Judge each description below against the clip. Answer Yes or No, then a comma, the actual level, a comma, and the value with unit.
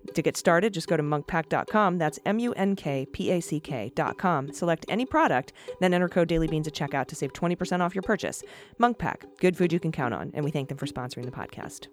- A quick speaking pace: Yes, fast, 230 wpm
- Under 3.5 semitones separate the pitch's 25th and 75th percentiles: No, average, 3.9 semitones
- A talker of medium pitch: Yes, medium, 170 Hz